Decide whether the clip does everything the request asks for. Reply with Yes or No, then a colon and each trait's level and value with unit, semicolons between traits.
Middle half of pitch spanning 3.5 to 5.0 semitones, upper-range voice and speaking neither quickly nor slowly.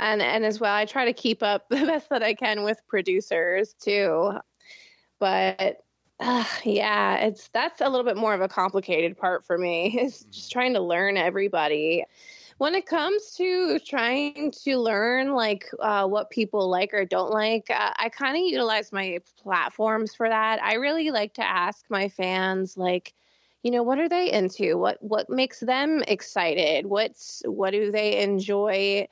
Yes: average, 4.2 semitones; high, 215 Hz; average, 175 wpm